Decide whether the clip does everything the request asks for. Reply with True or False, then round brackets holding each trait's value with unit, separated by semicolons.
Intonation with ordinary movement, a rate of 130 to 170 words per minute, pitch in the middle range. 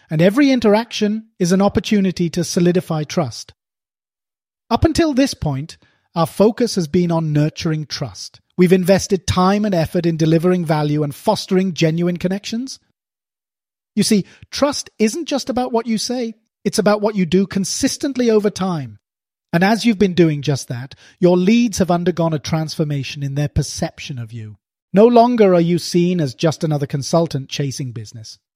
False (5.7 semitones; 165 wpm; 180 Hz)